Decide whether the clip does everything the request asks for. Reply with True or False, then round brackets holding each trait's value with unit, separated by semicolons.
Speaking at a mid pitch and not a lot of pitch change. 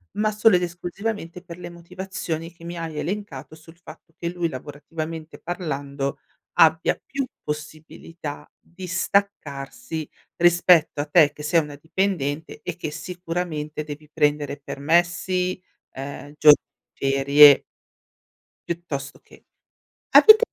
False (165 Hz; 3.0 semitones)